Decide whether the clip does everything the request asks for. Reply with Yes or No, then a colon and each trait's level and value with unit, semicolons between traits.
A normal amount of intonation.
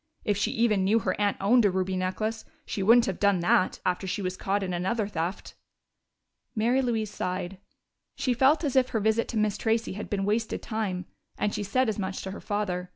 Yes: average, 3.0 semitones